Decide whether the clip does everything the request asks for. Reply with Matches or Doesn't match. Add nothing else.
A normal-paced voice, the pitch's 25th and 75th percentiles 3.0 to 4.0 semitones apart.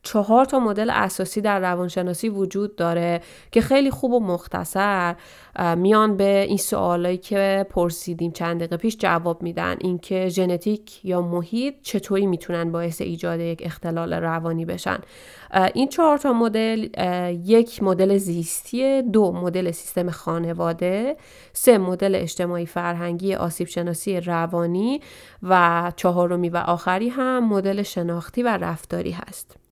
Matches